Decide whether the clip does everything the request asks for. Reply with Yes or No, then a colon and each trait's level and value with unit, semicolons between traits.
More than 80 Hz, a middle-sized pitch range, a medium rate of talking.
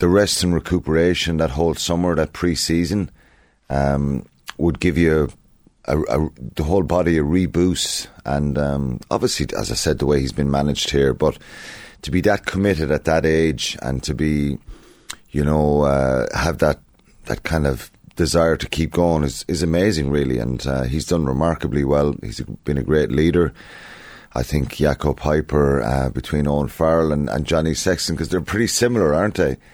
No: very low, 75 Hz; average, 3.1 semitones; average, 180 wpm